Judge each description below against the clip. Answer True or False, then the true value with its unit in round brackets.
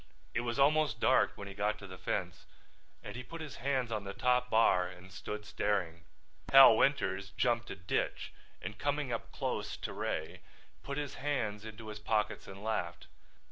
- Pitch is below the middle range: True (110 Hz)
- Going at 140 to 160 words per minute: False (180 wpm)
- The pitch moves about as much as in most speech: True (4.4 semitones)